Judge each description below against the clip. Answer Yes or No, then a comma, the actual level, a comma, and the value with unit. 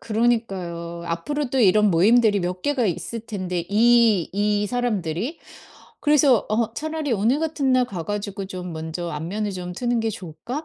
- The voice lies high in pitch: Yes, high, 210 Hz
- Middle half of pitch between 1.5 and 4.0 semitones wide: No, average, 5.1 semitones